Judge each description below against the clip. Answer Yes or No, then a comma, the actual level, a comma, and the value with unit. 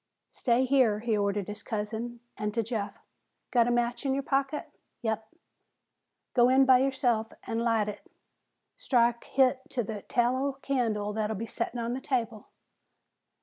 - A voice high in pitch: Yes, high, 235 Hz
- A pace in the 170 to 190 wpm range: No, average, 155 wpm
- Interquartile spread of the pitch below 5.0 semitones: Yes, average, 2.9 semitones